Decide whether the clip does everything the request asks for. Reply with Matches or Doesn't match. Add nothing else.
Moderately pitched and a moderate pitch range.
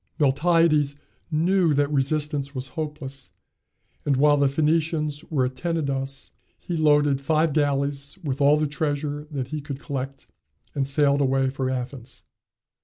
Doesn't match